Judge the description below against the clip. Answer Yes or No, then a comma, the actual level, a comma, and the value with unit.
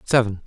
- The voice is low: Yes, low, 115 Hz